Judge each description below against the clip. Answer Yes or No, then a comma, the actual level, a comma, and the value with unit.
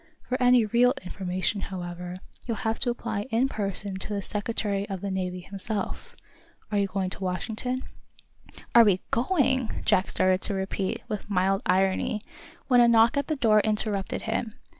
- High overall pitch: Yes, high, 205 Hz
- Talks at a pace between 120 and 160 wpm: No, average, 170 wpm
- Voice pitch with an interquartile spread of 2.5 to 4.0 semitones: Yes, average, 3.4 semitones